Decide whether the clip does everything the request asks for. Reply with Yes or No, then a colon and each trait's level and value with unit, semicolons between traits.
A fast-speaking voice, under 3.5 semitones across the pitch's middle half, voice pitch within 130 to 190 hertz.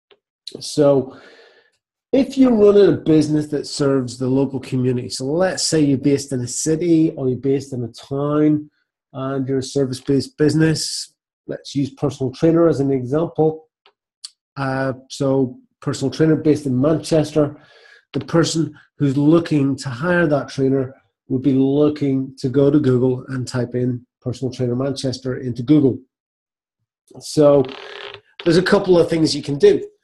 No: average, 155 wpm; average, 2.9 semitones; medium, 140 Hz